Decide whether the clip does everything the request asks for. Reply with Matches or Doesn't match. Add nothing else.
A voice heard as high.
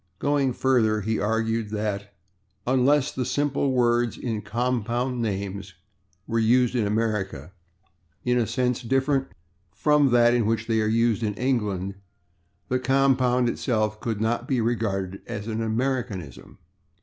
Doesn't match